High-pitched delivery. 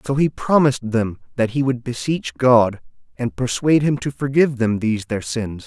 No: low, 120 Hz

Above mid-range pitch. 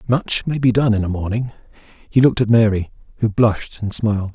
No: low, 110 Hz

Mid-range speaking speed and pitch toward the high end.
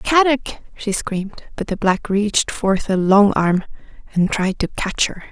Yes: average, 180 wpm; high, 200 Hz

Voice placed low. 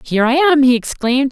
No: very high, 265 Hz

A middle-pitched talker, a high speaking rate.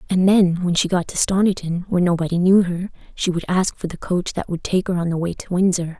Yes: medium, 180 Hz; fast, 260 wpm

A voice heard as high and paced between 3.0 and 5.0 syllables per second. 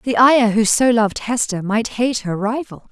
Yes: high, 225 Hz; 4.7 syllables/s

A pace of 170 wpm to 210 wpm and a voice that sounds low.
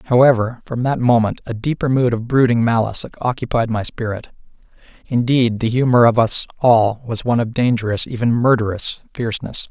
No: average, 160 wpm; low, 120 Hz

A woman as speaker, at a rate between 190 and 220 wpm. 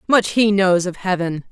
Yes: female; average, 200 wpm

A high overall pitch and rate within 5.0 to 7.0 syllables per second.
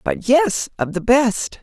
No: high, 225 Hz; 3.5 syllables/s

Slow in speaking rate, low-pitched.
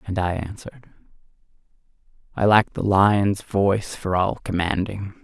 Yes: slow, 125 wpm; low, 100 Hz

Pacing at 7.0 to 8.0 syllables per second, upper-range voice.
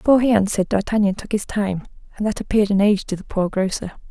Yes: 7.2 syllables/s; high, 205 Hz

